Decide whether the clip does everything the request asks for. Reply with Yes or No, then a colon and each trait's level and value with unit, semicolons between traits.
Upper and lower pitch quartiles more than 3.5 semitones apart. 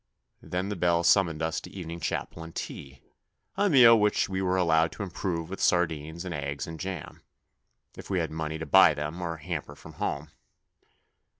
No: average, 2.8 semitones